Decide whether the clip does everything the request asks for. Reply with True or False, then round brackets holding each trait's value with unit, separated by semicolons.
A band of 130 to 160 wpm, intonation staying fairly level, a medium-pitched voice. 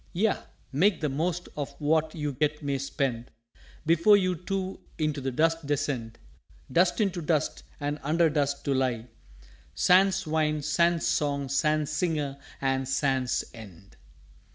False (140 wpm; 3.5 semitones; 150 Hz)